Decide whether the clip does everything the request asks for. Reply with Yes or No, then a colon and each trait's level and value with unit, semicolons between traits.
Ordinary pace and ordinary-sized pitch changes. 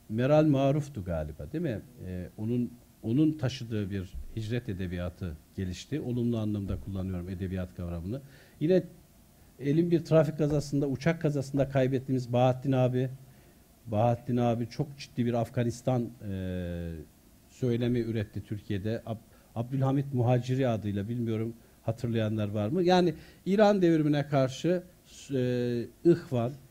Yes: average, 115 wpm; average, 5.0 semitones